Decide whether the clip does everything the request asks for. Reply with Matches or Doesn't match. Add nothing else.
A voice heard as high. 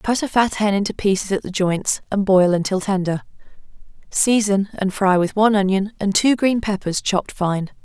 Matches